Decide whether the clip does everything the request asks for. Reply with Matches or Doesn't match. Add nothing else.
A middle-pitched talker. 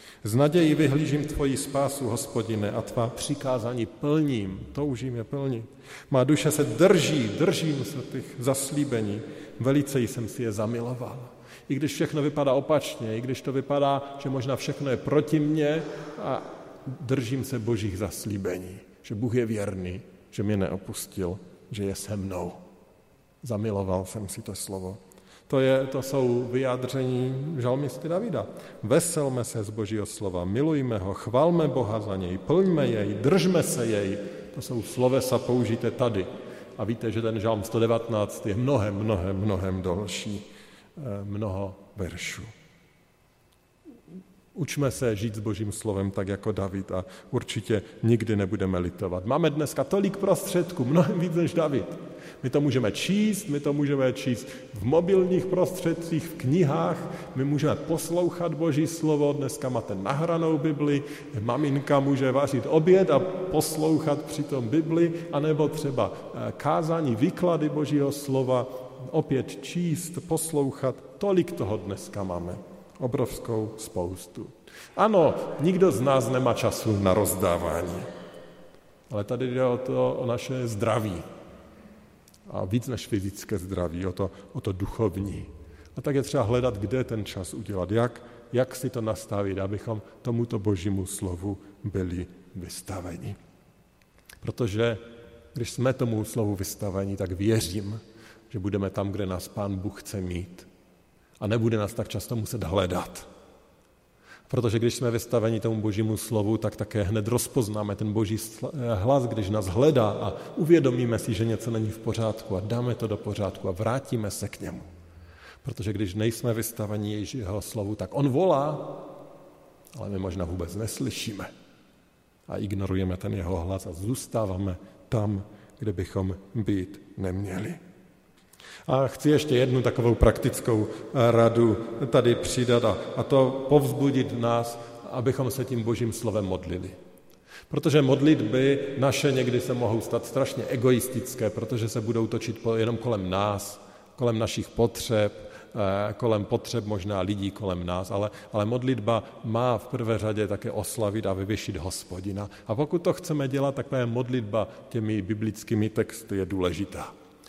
Doesn't match